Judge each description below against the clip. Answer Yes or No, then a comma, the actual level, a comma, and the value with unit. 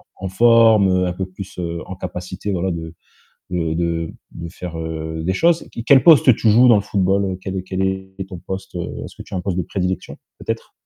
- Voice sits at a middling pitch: No, very low, 95 Hz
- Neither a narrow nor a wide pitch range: No, narrow, 2.3 semitones